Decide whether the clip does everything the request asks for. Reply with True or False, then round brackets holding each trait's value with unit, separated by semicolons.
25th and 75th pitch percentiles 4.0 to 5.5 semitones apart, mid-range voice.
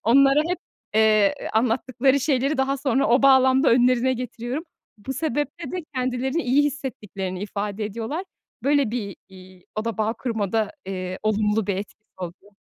False (4.3 semitones; 240 Hz)